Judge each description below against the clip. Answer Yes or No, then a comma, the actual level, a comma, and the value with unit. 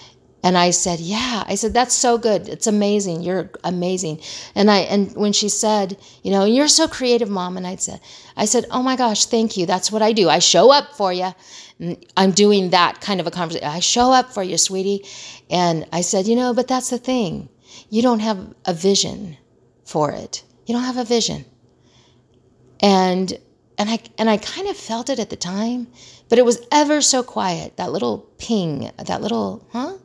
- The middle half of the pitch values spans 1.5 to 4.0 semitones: No, average, 4.7 semitones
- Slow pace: No, fast, 205 wpm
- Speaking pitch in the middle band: No, high, 205 Hz